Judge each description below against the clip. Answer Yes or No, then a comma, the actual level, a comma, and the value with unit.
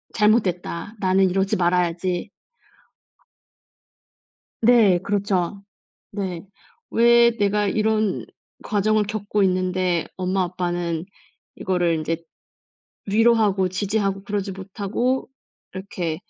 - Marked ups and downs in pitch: No, narrow, 2.6 semitones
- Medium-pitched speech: No, high, 195 Hz